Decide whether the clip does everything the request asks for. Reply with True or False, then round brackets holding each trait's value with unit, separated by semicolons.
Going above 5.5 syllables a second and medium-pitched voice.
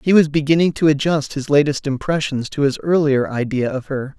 False (5.4 syllables/s; 145 Hz)